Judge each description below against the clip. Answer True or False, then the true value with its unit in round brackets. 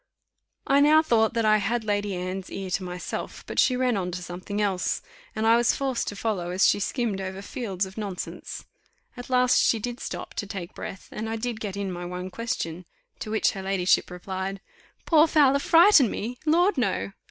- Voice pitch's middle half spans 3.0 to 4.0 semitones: False (4.5 semitones)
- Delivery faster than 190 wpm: True (200 wpm)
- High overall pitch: True (210 Hz)